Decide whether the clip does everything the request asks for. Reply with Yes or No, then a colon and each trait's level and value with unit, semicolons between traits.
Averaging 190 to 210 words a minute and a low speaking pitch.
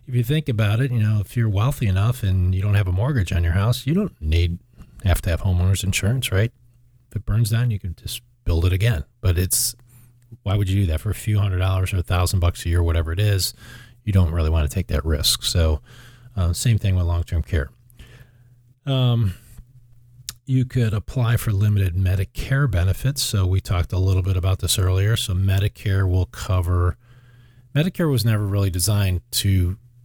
Yes: fast, 205 wpm; low, 105 Hz